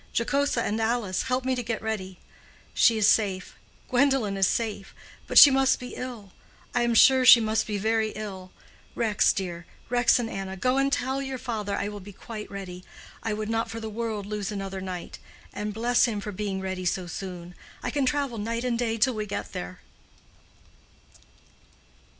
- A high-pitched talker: Yes, high, 220 Hz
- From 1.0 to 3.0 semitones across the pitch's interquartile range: No, average, 3.6 semitones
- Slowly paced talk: No, average, 180 wpm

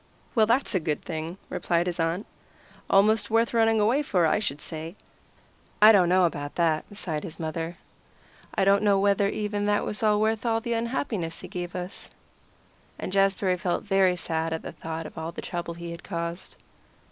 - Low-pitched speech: No, medium, 185 Hz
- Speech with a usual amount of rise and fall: Yes, average, 3.9 semitones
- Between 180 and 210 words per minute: Yes, average, 185 wpm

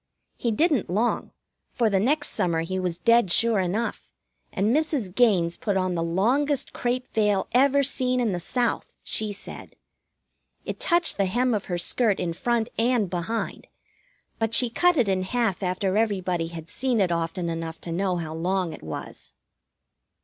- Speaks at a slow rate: No, average, 170 wpm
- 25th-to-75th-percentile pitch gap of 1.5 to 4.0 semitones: No, average, 5.3 semitones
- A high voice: Yes, high, 205 Hz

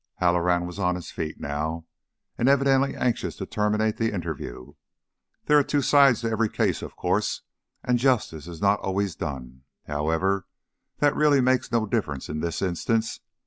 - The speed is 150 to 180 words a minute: Yes, average, 165 wpm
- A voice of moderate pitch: No, low, 100 Hz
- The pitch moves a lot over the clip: Yes, wide, 6.5 semitones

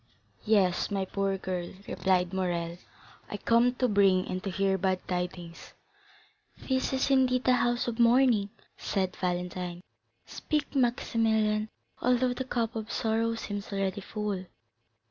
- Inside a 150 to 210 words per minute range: No, slow, 135 wpm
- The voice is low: No, high, 205 Hz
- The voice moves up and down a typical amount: Yes, average, 4.3 semitones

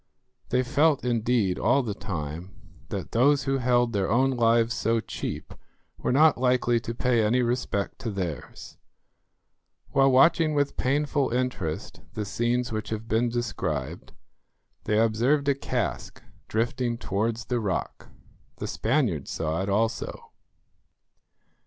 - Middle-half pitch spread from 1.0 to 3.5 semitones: Yes, average, 3.2 semitones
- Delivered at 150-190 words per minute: No, slow, 135 wpm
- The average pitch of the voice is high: No, low, 120 Hz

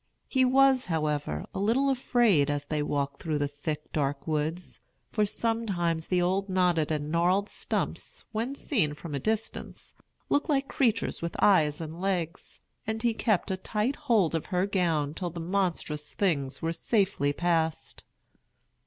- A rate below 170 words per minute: Yes, average, 160 wpm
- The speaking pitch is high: No, medium, 175 Hz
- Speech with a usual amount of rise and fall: No, wide, 5.9 semitones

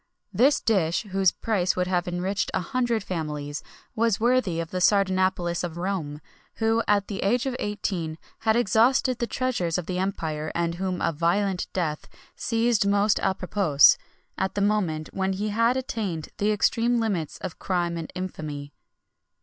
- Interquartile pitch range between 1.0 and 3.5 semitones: No, average, 4.2 semitones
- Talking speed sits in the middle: Yes, average, 165 wpm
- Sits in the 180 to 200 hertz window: Yes, high, 190 Hz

